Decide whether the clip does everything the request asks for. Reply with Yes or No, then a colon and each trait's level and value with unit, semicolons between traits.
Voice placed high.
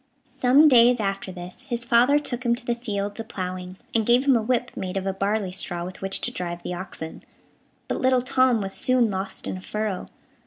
Yes: high, 215 Hz